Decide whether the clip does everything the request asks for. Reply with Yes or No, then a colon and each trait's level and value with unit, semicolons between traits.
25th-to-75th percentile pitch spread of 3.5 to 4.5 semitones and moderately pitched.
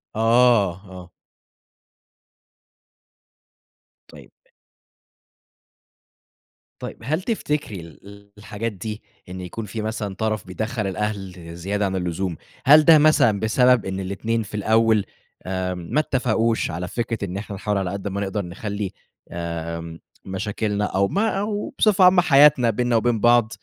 No: average, 3.8 semitones; low, 105 Hz